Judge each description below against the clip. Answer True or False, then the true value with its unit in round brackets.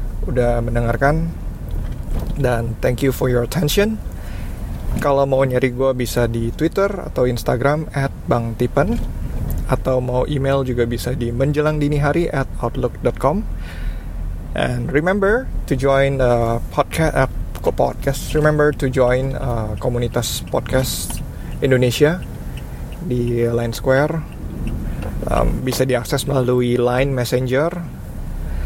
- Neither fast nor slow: True (115 wpm)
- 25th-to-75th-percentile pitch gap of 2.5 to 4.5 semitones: True (2.9 semitones)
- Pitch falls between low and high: False (125 Hz)